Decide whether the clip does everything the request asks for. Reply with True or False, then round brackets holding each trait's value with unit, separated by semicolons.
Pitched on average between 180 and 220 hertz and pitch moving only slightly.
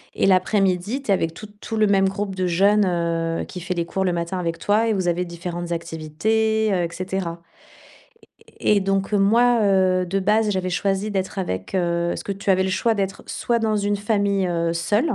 False (190 Hz; 3.0 semitones)